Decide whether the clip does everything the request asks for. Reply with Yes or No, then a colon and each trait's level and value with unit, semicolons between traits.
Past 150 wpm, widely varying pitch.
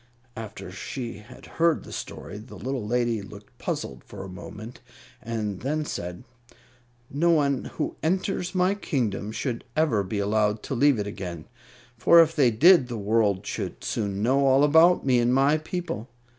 Yes: average, 170 wpm; wide, 6.2 semitones